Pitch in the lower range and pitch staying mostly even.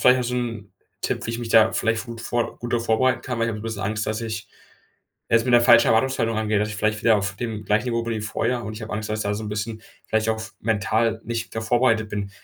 Yes: low, 110 Hz; narrow, 1.5 semitones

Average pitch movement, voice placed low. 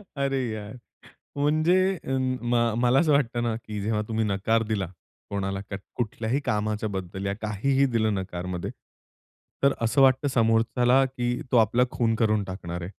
Yes: average, 4.0 semitones; low, 115 Hz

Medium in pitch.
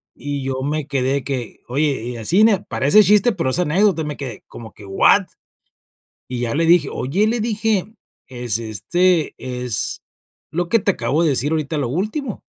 Yes: medium, 145 Hz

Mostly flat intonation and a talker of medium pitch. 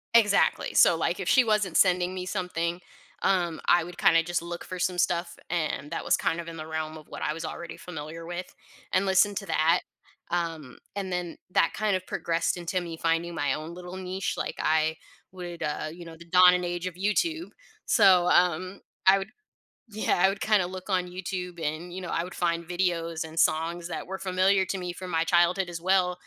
Yes: narrow, 1.9 semitones; medium, 175 Hz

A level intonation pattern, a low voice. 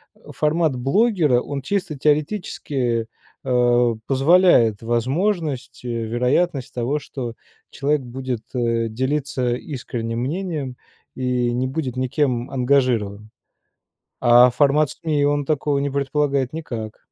No: average, 3.5 semitones; low, 130 Hz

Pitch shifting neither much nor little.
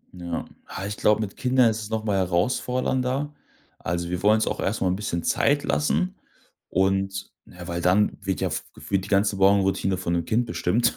Yes: average, 3.4 semitones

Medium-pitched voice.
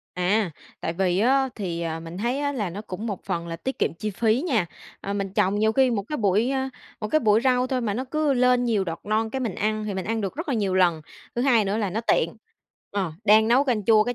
No: high, 215 Hz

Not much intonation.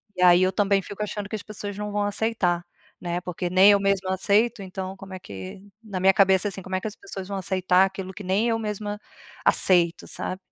Yes: narrow, 1.8 semitones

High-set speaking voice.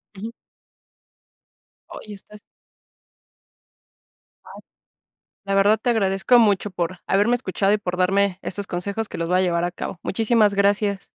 Yes: high, 200 Hz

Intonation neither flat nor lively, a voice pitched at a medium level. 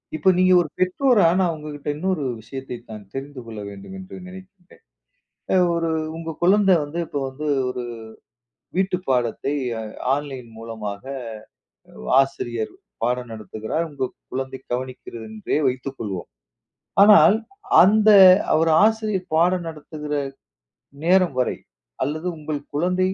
No: wide, 6.4 semitones; medium, 150 Hz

